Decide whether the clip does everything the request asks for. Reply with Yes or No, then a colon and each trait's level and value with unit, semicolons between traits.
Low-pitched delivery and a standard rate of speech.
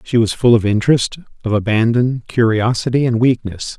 Yes: low, 115 Hz; average, 160 wpm